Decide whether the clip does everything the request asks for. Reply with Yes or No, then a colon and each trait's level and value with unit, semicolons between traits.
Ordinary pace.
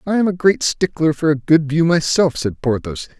No: fast, 225 wpm